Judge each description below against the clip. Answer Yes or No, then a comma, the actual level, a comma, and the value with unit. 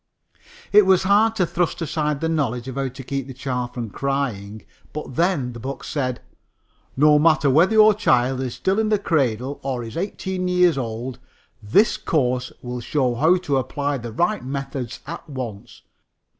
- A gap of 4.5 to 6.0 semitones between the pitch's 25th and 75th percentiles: Yes, wide, 5.6 semitones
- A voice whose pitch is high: No, medium, 140 Hz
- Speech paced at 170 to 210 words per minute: Yes, average, 175 wpm